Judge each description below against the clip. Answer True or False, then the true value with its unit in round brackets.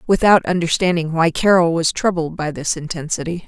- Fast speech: False (155 wpm)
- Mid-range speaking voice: True (170 Hz)